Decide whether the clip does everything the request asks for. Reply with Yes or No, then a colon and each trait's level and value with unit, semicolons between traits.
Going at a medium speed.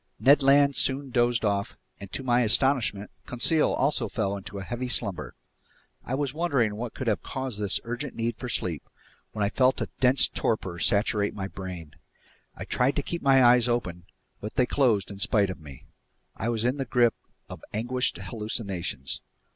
Yes: average, 180 wpm